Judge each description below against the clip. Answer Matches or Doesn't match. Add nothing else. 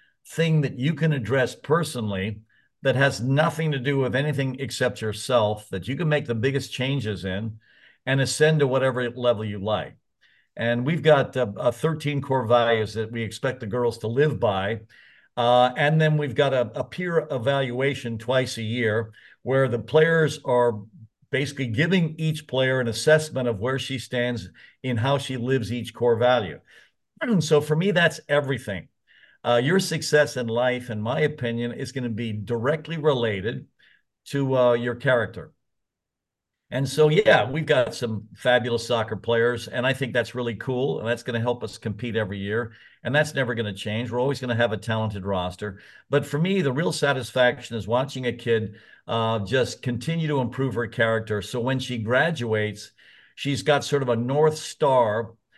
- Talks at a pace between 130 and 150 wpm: Doesn't match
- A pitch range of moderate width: Matches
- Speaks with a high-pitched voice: Doesn't match